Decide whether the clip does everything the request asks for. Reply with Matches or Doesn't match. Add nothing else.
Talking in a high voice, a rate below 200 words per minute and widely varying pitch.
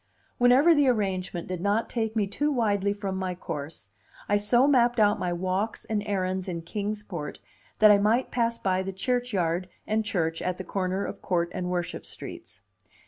Doesn't match